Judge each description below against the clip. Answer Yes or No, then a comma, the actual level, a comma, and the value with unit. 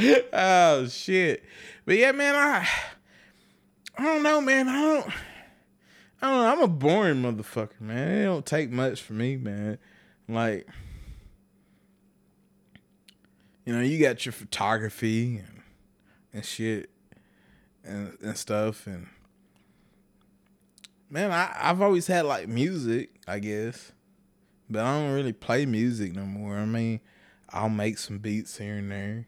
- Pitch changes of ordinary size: No, wide, 8.1 semitones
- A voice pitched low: Yes, low, 115 Hz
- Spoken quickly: No, slow, 135 wpm